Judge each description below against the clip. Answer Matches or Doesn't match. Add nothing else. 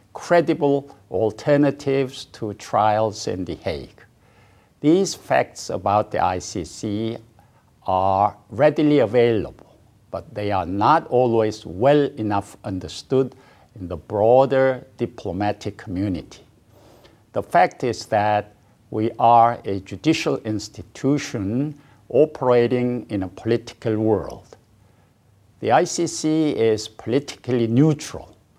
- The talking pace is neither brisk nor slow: Doesn't match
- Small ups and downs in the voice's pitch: Doesn't match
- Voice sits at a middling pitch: Doesn't match